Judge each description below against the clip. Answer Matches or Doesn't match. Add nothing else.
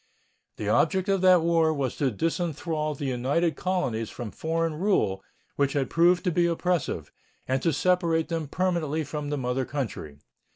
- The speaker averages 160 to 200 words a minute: Matches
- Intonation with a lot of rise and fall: Doesn't match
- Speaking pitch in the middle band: Matches